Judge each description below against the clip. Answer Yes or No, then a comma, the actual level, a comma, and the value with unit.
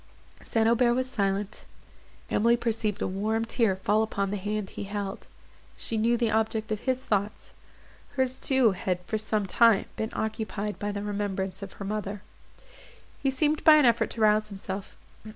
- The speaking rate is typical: Yes, average, 170 wpm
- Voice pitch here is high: Yes, high, 215 Hz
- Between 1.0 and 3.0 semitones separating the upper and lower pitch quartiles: Yes, narrow, 2.5 semitones